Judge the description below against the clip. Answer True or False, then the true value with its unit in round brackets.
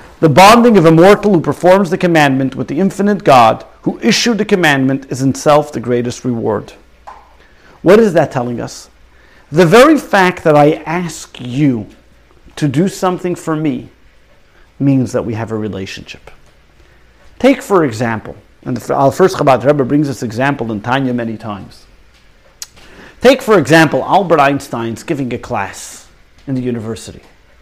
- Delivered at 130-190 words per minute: True (155 wpm)